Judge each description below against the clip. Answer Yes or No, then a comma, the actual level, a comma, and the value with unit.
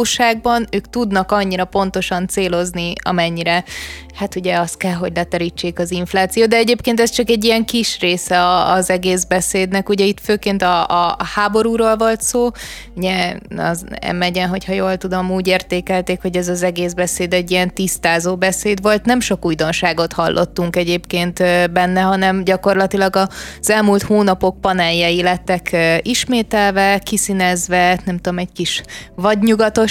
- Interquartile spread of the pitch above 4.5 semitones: No, narrow, 2.5 semitones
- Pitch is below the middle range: No, medium, 185 Hz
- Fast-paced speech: No, average, 140 wpm